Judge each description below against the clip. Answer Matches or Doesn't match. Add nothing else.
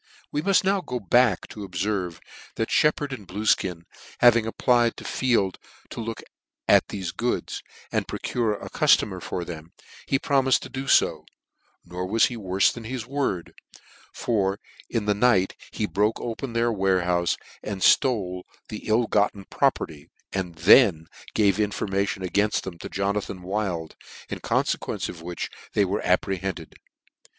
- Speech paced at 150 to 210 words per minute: Matches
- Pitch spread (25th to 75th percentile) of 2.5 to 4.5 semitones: Matches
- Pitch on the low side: Matches